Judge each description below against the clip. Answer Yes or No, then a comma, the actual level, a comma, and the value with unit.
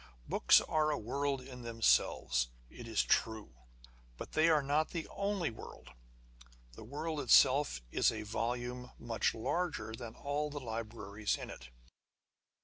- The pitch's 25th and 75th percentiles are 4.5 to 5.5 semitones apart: Yes, average, 4.9 semitones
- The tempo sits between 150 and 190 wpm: No, average, 140 wpm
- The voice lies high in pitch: No, low, 125 Hz